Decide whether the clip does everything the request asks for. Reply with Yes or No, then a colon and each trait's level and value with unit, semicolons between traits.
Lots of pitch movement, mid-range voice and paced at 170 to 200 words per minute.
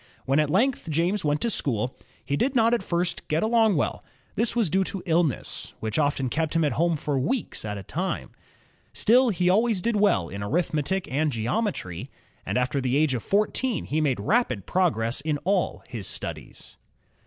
Yes: wide, 7.1 semitones; medium, 160 Hz; average, 190 wpm